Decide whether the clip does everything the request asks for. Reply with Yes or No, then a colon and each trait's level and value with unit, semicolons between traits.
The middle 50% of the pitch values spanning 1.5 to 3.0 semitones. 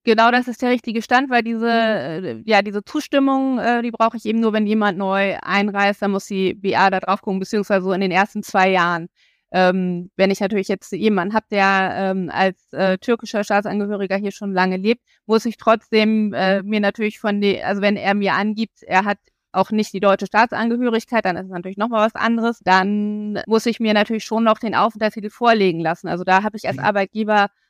Yes: narrow, 2.5 semitones